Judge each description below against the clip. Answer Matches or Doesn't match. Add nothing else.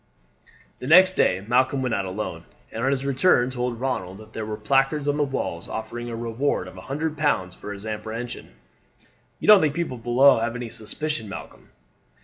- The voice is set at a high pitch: Doesn't match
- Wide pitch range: Doesn't match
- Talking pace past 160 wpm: Matches